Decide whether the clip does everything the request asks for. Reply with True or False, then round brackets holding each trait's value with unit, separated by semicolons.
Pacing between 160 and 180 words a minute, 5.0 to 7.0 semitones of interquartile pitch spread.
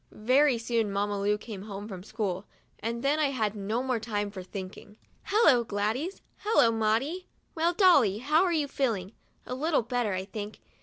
True (175 wpm; 5.3 semitones)